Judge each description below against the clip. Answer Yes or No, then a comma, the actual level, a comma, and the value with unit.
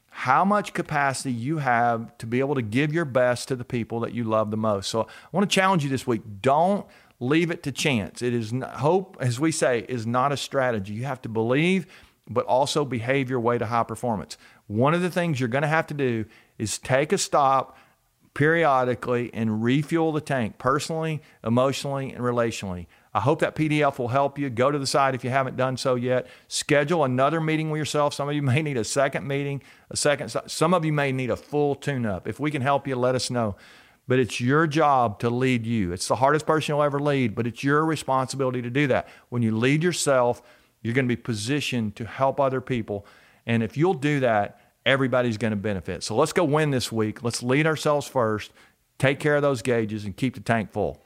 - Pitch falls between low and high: No, low, 130 Hz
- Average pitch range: Yes, average, 3.7 semitones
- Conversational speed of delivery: No, fast, 225 wpm